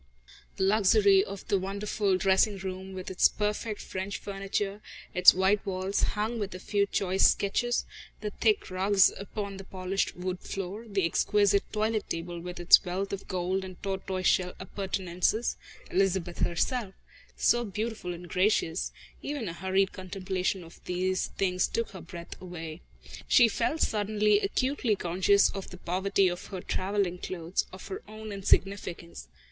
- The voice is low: No, high, 195 Hz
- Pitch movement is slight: Yes, narrow, 2.0 semitones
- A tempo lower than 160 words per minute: Yes, average, 150 wpm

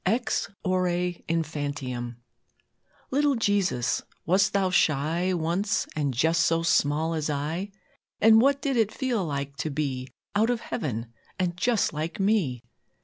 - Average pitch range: No, wide, 5.8 semitones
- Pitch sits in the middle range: Yes, medium, 170 Hz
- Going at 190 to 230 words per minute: No, average, 140 wpm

